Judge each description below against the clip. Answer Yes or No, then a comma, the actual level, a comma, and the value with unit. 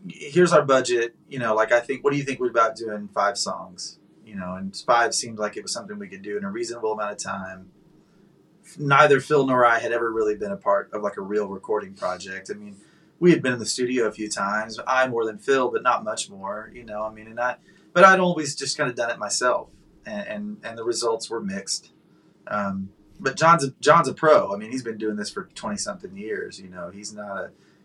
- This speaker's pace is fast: Yes, fast, 245 wpm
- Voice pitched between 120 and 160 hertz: Yes, low, 135 Hz